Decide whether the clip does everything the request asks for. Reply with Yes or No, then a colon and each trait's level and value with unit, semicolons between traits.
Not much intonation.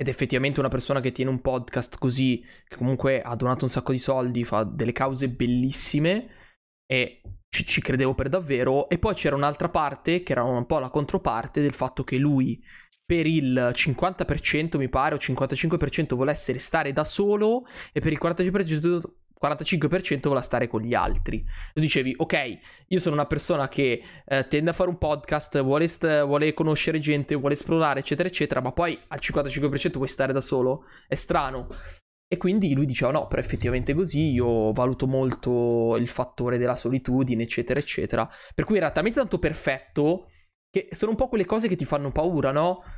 No: average, 4.0 semitones